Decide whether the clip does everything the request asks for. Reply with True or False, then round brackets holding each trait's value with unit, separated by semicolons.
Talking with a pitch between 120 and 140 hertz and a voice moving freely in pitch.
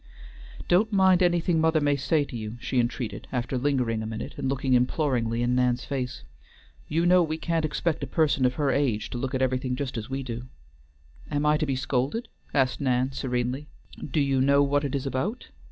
False (135 Hz; 3.3 semitones)